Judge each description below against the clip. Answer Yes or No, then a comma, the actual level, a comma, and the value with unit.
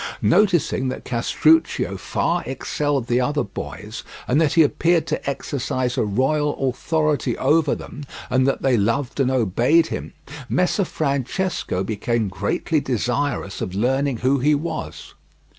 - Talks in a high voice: No, low, 135 Hz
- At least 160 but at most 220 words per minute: No, average, 140 wpm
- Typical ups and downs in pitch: Yes, average, 3.8 semitones